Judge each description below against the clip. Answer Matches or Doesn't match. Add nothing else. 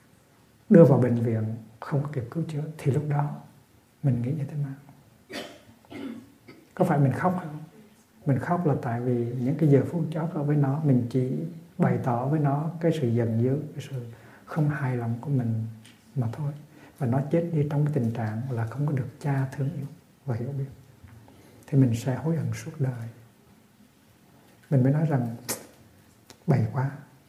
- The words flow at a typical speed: Matches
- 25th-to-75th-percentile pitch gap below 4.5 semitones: Matches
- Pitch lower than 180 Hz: Matches